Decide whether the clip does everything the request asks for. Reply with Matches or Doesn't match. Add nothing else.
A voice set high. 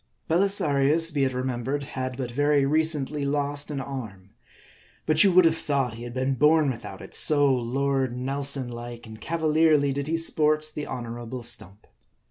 Doesn't match